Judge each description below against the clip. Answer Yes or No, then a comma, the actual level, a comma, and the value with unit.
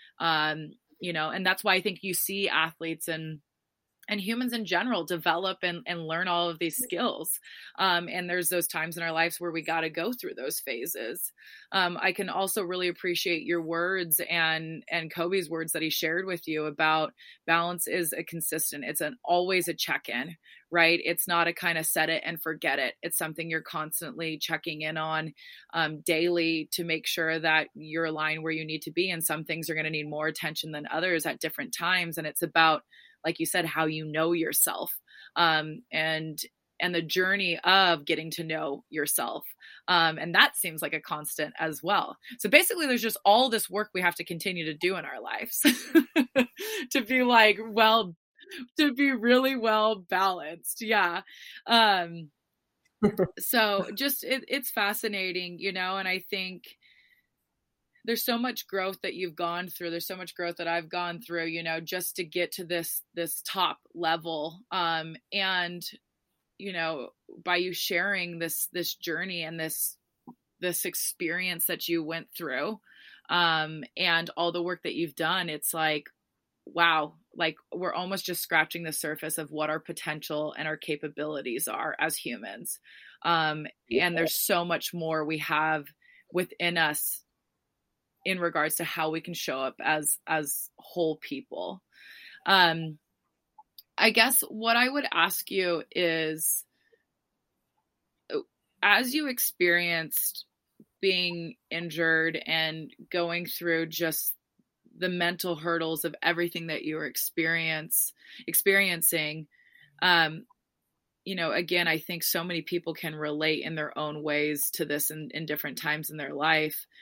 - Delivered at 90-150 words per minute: No, average, 165 wpm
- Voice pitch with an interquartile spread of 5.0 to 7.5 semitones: No, average, 2.9 semitones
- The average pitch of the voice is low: No, medium, 170 Hz